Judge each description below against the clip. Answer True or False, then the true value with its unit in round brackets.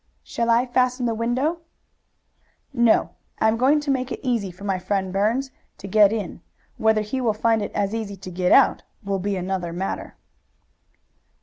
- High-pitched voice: True (220 Hz)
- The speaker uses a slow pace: False (180 wpm)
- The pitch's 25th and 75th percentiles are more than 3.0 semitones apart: True (3.8 semitones)